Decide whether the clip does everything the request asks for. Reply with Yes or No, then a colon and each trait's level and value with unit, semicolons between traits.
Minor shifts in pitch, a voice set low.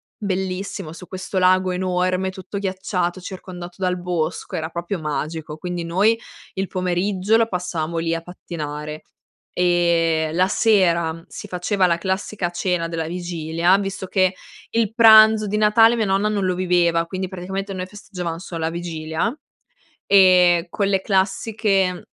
No: narrow, 2.3 semitones; medium, 180 Hz